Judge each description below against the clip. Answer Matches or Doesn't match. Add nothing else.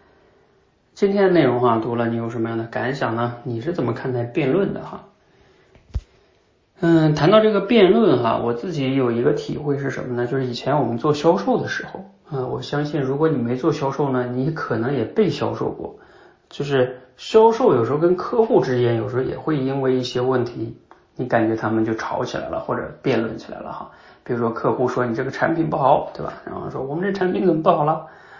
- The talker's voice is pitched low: Matches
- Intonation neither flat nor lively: Matches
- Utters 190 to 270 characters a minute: Doesn't match